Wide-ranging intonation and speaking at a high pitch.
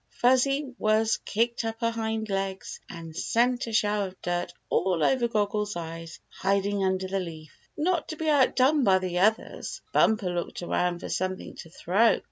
No: average, 4.2 semitones; high, 205 Hz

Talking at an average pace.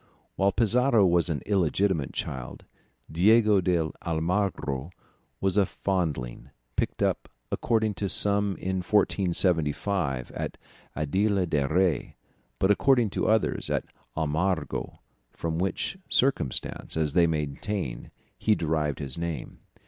No: slow, 120 wpm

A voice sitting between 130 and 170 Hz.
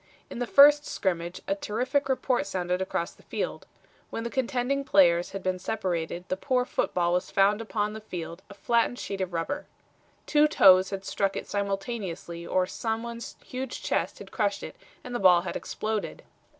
No: high, 200 Hz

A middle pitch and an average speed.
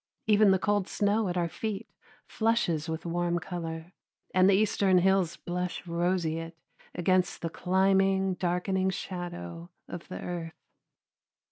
No: medium, 180 Hz; slow, 130 wpm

